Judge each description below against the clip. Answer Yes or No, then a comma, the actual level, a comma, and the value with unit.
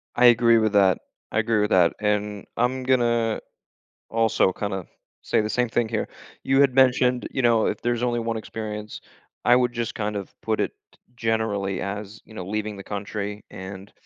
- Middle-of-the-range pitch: No, low, 110 Hz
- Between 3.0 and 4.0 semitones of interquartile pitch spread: No, narrow, 2.5 semitones